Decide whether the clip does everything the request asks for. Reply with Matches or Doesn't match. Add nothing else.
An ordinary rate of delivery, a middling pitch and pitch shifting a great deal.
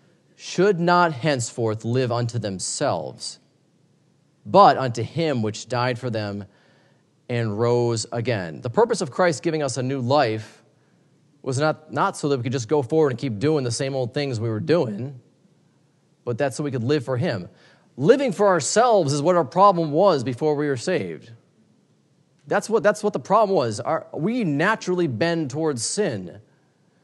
Matches